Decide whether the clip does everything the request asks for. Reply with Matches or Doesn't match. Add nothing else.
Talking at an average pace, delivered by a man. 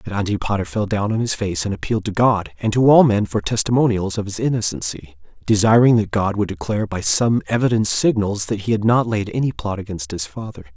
Doesn't match